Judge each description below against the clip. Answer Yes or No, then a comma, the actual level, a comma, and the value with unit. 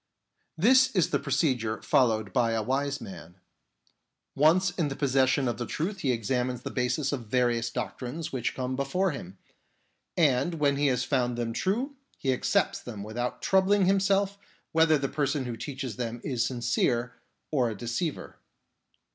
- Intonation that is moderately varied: Yes, average, 4.6 semitones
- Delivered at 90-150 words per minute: No, average, 160 wpm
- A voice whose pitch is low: Yes, low, 130 Hz